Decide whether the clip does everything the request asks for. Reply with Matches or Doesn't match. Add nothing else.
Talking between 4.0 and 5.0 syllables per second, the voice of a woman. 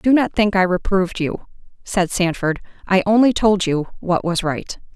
Matches